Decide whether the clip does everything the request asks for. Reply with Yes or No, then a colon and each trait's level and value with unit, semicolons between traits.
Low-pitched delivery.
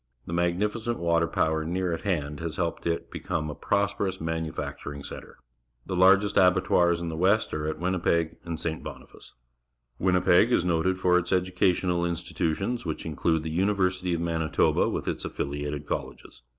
Yes: very low, 85 Hz